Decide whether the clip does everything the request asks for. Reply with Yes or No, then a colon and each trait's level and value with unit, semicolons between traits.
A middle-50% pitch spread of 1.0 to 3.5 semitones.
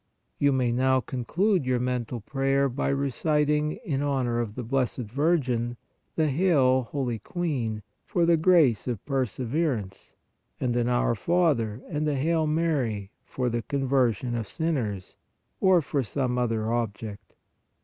No: average, 4.1 semitones